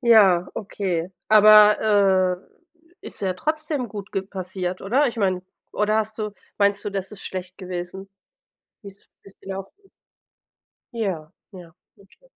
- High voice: Yes, high, 195 Hz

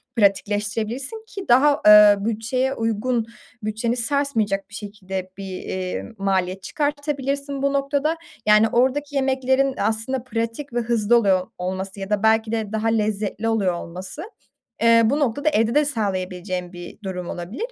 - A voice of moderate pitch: No, high, 225 Hz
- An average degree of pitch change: Yes, average, 5.0 semitones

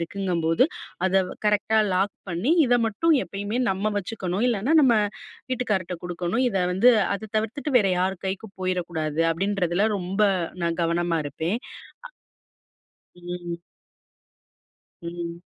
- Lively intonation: No, average, 3.8 semitones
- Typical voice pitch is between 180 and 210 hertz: Yes, high, 190 Hz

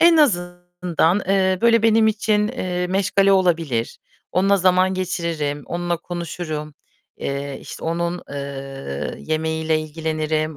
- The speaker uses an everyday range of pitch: Yes, average, 3.3 semitones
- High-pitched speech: No, medium, 175 Hz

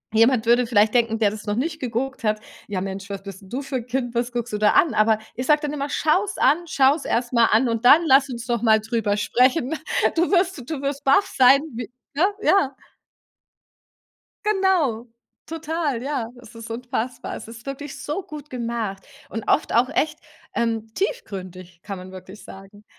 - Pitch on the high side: Yes, high, 240 Hz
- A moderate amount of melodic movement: Yes, average, 4.6 semitones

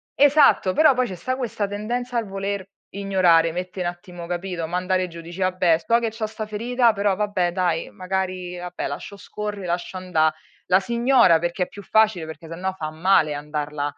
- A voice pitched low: No, medium, 185 Hz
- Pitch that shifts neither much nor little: Yes, average, 3.3 semitones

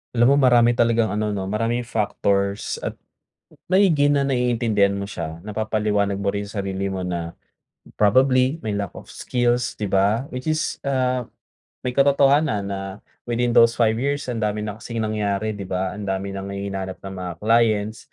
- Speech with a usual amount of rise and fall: Yes, average, 3.7 semitones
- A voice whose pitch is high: No, low, 110 Hz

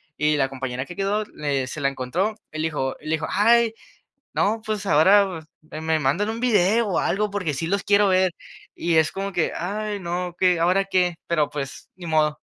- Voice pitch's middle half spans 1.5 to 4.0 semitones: No, average, 4.7 semitones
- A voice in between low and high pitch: Yes, medium, 175 Hz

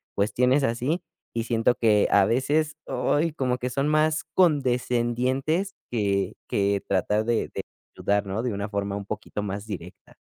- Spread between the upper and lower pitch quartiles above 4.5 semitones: Yes, average, 5.0 semitones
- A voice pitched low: Yes, low, 120 Hz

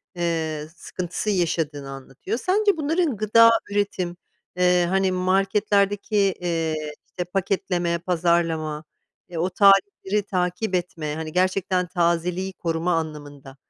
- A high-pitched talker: No, medium, 180 Hz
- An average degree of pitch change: Yes, average, 3.2 semitones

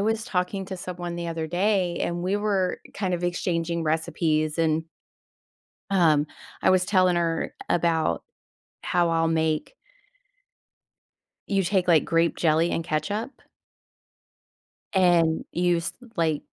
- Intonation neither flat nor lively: No, narrow, 2.2 semitones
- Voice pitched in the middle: Yes, medium, 175 Hz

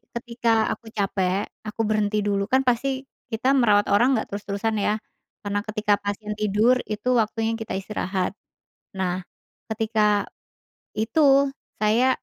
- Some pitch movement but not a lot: No, narrow, 2.3 semitones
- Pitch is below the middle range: No, high, 215 Hz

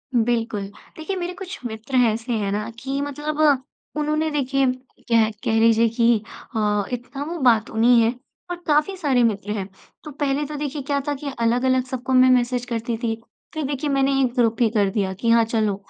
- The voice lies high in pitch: Yes, high, 245 Hz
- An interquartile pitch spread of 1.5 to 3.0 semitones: No, average, 4.0 semitones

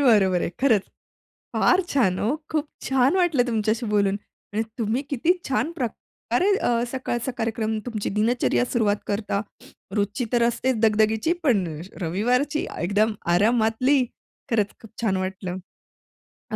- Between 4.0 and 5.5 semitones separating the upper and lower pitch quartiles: No, average, 3.6 semitones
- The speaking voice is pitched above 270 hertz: No, high, 225 Hz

